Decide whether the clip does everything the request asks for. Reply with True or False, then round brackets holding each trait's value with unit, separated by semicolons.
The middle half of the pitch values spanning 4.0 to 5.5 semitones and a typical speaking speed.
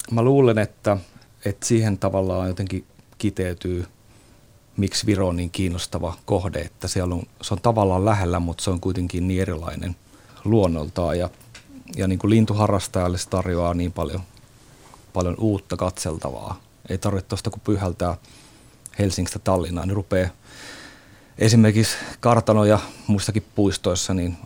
False (3.4 semitones; 135 wpm)